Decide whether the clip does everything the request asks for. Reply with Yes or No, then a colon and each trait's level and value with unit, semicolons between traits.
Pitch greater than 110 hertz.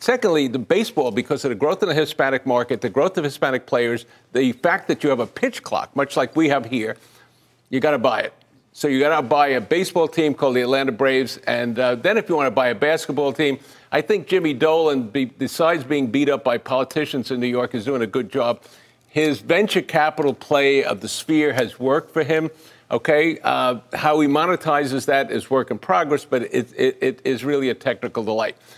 Yes: medium, 140 Hz